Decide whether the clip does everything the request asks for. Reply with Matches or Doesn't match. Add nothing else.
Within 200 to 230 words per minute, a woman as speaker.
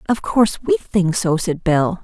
Matches